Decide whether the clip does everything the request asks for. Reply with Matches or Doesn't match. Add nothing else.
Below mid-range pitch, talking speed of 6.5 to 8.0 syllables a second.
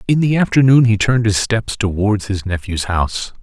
Doesn't match